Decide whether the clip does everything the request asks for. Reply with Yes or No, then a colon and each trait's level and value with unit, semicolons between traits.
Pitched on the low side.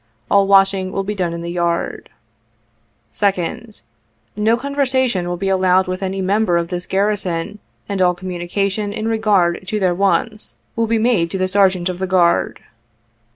No: high, 190 Hz